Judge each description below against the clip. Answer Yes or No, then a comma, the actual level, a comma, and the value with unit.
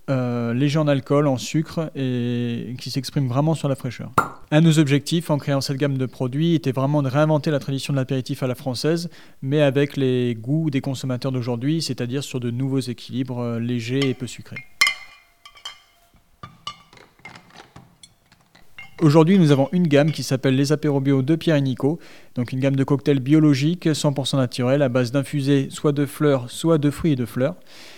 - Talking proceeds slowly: No, average, 180 wpm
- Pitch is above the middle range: No, medium, 140 Hz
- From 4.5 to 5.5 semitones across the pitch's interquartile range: No, narrow, 2.5 semitones